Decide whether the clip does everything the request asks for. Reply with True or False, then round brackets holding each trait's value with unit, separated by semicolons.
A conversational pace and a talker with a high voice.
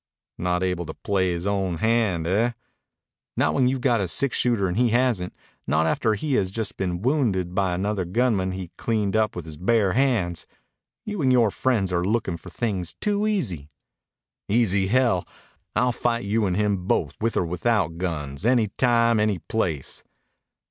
False (175 wpm; 100 Hz)